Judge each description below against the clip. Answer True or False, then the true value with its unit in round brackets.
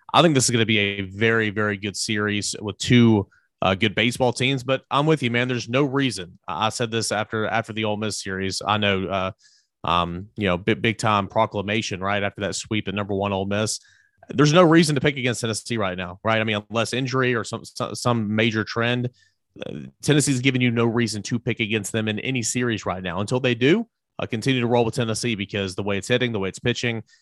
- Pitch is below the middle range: True (110 Hz)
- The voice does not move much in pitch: False (3.2 semitones)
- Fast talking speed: True (230 wpm)